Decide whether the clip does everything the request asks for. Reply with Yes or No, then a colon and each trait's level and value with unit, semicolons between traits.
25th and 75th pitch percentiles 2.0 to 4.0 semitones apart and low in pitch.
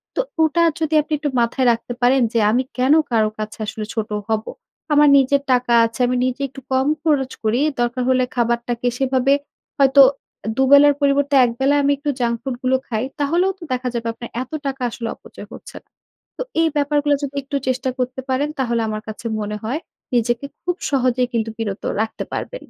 No: average, 3.1 semitones; very high, 255 Hz